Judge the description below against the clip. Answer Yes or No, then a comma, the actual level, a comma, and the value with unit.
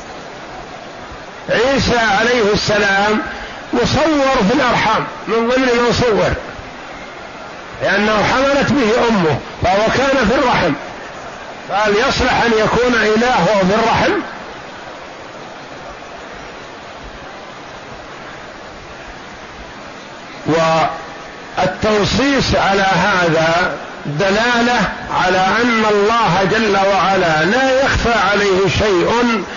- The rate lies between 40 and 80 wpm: Yes, average, 75 wpm